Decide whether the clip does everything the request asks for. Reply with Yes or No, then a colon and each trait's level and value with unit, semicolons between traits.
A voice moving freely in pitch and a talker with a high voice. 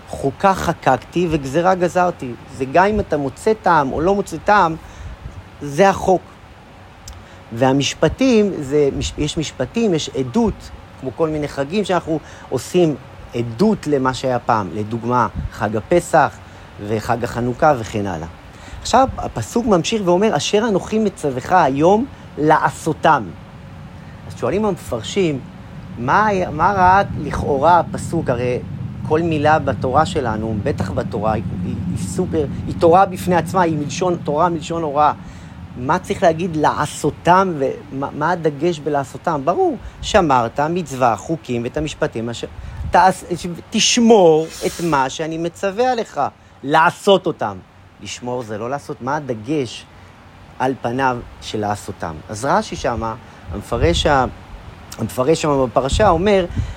No: wide, 7.8 semitones; medium, 140 Hz